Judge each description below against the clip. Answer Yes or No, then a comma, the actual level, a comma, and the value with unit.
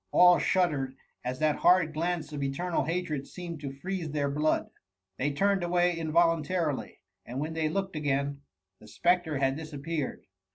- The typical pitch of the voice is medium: Yes, medium, 155 Hz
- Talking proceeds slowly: No, average, 155 wpm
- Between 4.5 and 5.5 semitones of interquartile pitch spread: No, average, 3.7 semitones